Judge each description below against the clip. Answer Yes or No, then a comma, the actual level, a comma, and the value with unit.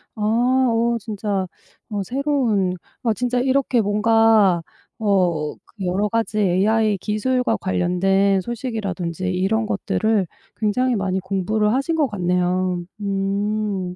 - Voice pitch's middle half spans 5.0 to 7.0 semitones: No, average, 3.2 semitones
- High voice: Yes, high, 210 Hz